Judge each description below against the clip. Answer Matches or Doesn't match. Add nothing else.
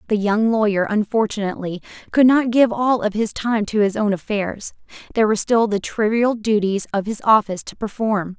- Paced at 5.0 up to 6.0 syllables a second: Matches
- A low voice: Doesn't match